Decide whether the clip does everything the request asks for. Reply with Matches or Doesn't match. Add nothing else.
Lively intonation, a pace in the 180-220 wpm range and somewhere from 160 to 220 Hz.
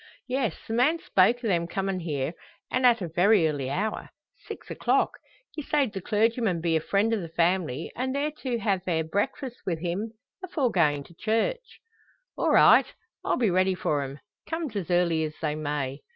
Matches